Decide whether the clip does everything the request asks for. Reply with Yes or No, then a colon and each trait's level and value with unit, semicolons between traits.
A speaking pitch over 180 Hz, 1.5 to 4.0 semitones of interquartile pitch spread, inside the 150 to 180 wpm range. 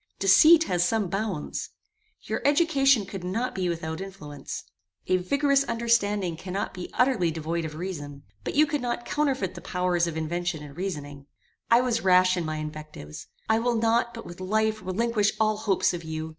No: high, 190 Hz; wide, 5.4 semitones; average, 175 wpm